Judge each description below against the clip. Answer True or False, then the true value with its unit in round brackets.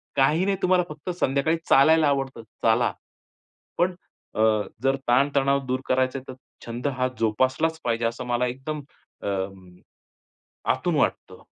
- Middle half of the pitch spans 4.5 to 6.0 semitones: False (3.6 semitones)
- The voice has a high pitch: False (135 Hz)